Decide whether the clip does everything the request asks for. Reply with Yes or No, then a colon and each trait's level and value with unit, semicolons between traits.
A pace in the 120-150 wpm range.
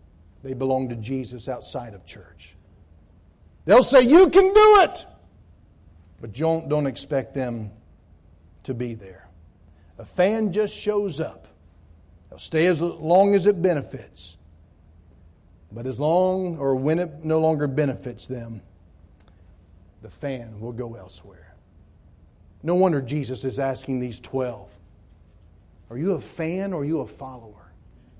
Yes: slow, 135 wpm